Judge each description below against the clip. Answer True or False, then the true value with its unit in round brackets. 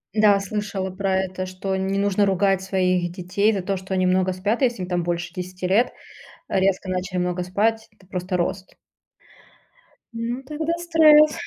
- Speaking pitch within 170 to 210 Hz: True (190 Hz)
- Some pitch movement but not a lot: False (2.3 semitones)